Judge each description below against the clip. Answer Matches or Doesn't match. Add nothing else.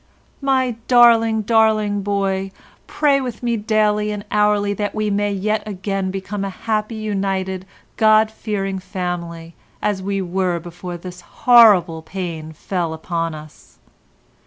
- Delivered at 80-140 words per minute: Matches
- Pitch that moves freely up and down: Doesn't match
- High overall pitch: Matches